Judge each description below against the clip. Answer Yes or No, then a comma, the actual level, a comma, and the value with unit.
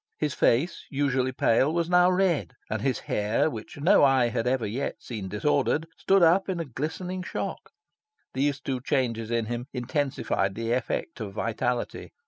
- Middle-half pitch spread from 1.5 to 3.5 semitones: No, average, 5.1 semitones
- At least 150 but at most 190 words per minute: Yes, average, 165 wpm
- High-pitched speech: No, low, 130 Hz